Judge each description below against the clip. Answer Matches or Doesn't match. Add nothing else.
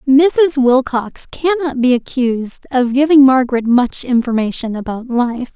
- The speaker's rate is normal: Doesn't match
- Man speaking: Doesn't match